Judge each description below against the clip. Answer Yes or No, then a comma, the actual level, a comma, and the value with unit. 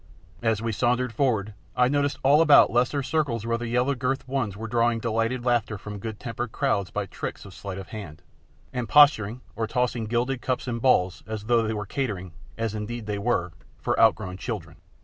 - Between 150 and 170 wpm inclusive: No, average, 195 wpm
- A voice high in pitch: No, low, 115 Hz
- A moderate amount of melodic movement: Yes, average, 3.1 semitones